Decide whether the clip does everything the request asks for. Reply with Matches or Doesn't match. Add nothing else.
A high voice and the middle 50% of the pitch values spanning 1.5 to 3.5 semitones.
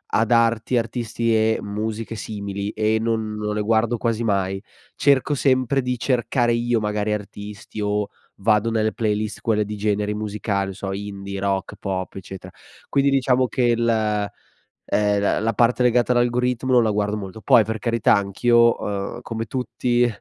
Doesn't match